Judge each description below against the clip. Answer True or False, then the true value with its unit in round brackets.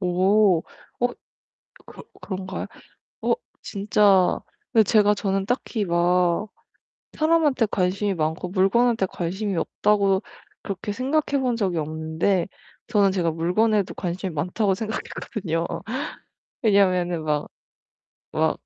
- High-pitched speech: True (195 Hz)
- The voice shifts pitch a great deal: False (3.3 semitones)